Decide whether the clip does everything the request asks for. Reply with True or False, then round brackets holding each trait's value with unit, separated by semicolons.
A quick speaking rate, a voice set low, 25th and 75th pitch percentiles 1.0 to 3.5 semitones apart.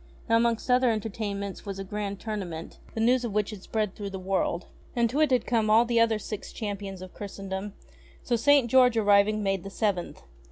False (210 wpm; 210 Hz; 2.8 semitones)